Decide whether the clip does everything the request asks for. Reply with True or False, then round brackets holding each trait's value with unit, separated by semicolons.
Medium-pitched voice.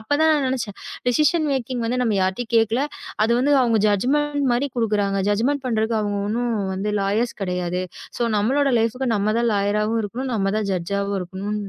False (225 Hz)